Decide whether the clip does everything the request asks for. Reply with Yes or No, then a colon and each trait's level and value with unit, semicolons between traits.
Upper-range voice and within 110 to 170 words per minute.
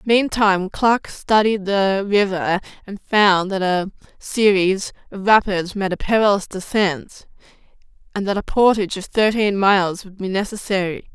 Yes: high, 200 Hz; average, 140 wpm